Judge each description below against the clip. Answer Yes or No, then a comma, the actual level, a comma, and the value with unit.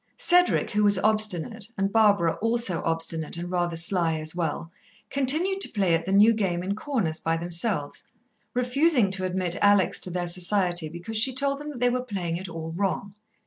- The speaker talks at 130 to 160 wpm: No, average, 185 wpm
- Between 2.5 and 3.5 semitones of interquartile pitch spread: No, average, 4.9 semitones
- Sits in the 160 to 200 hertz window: Yes, high, 190 Hz